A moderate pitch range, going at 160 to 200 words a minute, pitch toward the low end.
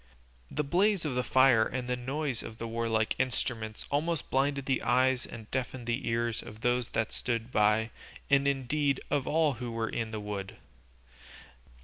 Yes: average, 3.4 semitones; average, 170 wpm; low, 125 Hz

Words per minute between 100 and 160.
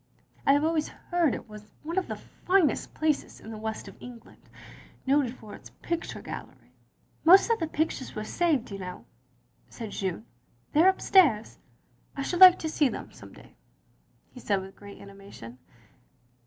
No: average, 180 wpm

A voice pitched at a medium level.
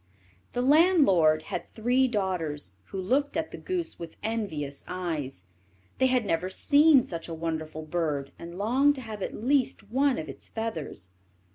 No: high, 195 Hz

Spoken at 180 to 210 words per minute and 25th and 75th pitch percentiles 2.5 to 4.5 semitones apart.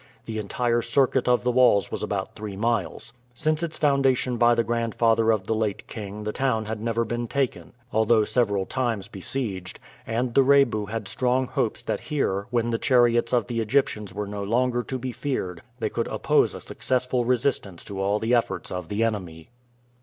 Yes: average, 190 wpm; average, 3.0 semitones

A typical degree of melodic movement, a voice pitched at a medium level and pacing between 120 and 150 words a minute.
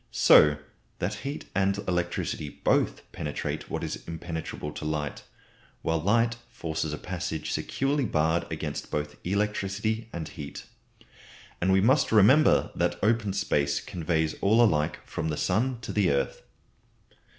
No: average, 5.0 semitones; very low, 90 Hz; average, 140 wpm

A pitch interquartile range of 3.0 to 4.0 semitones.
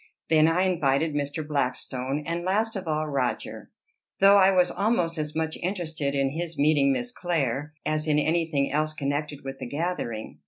Yes: average, 3.5 semitones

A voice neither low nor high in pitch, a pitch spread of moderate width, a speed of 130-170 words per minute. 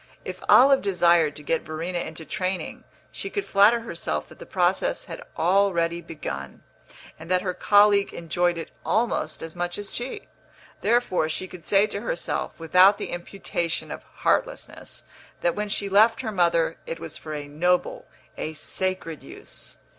Yes: medium, 180 Hz; average, 3.7 semitones; average, 160 wpm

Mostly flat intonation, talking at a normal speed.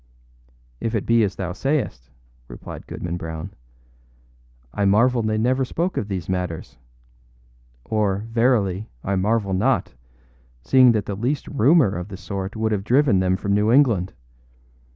No: average, 4.0 semitones; average, 150 wpm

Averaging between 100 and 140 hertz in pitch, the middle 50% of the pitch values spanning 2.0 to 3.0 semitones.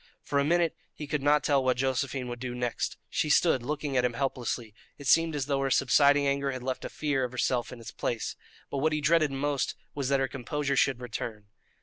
Yes: low, 135 Hz; average, 2.7 semitones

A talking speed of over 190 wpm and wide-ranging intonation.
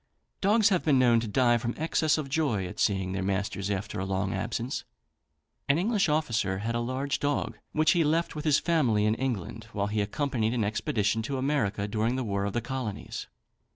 Yes: average, 200 wpm; wide, 5.9 semitones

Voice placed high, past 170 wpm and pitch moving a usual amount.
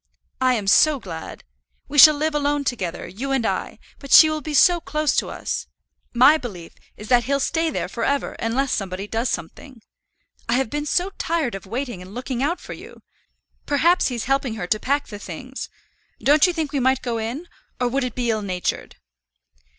Yes: very high, 260 Hz; average, 200 wpm; average, 4.6 semitones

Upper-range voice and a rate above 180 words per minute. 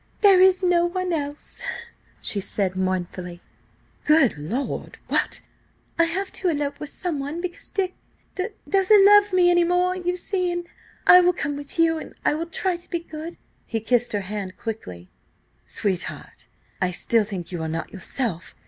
No: very high, 315 Hz; average, 155 wpm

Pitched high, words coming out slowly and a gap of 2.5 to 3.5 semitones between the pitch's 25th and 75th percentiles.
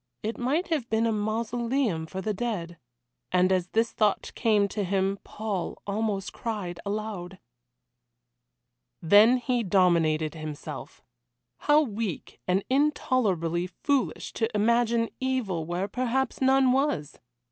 No: high, 215 Hz; slow, 125 wpm; average, 4.8 semitones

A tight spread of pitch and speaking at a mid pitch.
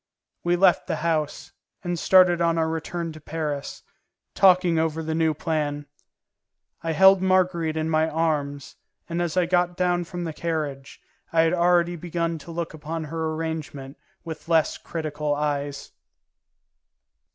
Yes: narrow, 2.0 semitones; medium, 165 Hz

